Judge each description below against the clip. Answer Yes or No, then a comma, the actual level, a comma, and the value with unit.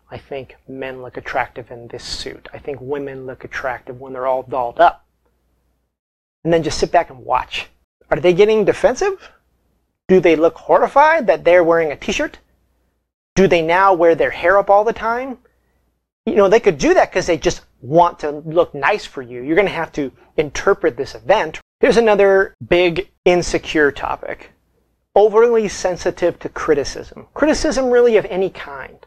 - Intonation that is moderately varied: No, wide, 7.2 semitones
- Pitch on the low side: No, medium, 175 Hz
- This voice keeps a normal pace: Yes, average, 175 wpm